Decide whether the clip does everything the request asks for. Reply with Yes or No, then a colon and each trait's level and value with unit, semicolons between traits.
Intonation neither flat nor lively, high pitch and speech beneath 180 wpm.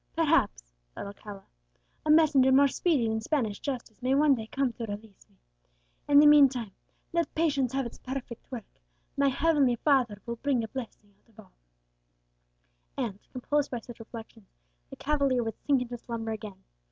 Yes: average, 4.0 semitones; high, 245 Hz; average, 170 wpm